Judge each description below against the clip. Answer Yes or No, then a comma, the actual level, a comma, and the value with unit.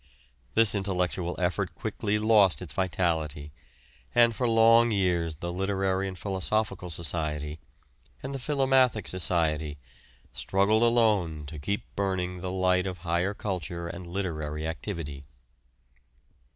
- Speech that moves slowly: Yes, slow, 120 wpm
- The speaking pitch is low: Yes, very low, 95 Hz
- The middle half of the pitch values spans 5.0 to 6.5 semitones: No, average, 3.8 semitones